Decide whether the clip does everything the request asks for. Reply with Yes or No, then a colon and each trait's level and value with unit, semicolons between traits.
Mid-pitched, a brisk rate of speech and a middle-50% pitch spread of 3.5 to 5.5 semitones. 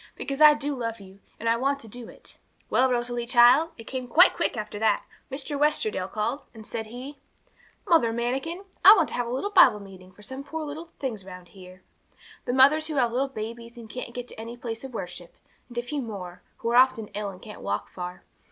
No: high, 240 Hz; fast, 225 wpm; average, 4.3 semitones